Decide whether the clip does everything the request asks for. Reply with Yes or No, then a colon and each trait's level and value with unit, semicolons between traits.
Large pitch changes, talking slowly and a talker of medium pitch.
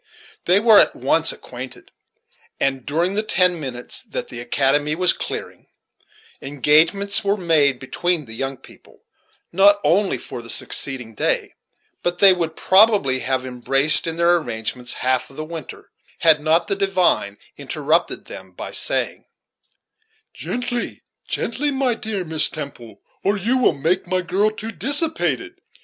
No: wide, 6.6 semitones; average, 145 wpm; medium, 165 Hz